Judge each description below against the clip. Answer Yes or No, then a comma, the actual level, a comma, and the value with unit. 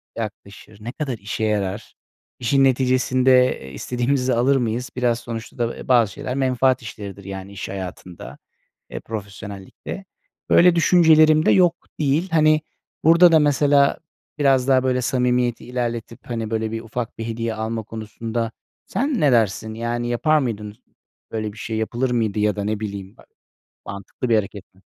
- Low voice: Yes, low, 120 Hz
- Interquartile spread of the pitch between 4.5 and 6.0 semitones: No, average, 3.5 semitones